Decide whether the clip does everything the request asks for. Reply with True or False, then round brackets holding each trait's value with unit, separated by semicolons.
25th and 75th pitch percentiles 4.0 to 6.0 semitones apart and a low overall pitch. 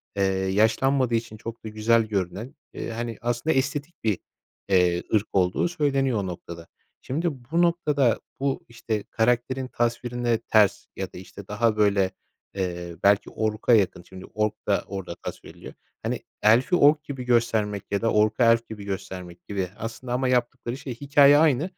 True (4.3 semitones; 115 Hz)